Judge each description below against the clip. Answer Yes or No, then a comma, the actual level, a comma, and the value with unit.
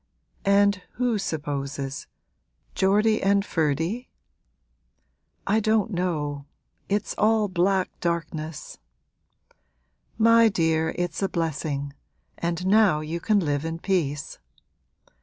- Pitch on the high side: No, medium, 175 Hz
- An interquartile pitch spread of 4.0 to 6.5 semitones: Yes, average, 4.6 semitones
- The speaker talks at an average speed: No, slow, 100 wpm